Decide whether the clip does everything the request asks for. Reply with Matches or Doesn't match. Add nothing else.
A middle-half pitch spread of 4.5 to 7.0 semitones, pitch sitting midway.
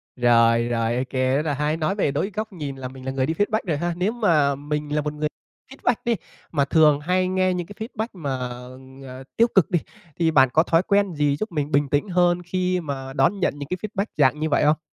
Matches